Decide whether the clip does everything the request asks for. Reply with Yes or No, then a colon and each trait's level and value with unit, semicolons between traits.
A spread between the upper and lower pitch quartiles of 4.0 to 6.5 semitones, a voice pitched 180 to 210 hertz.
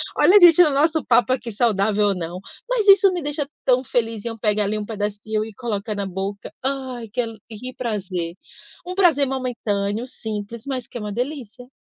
No: average, 4.4 semitones; high, 230 Hz